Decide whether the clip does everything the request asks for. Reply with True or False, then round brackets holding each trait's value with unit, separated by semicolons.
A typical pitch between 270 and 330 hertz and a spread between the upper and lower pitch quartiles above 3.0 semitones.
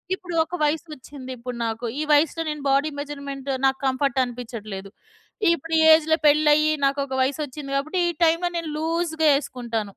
True (285 Hz; 3.5 semitones)